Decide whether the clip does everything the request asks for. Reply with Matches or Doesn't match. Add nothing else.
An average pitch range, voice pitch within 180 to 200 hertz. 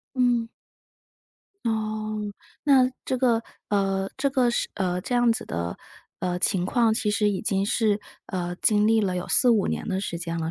Doesn't match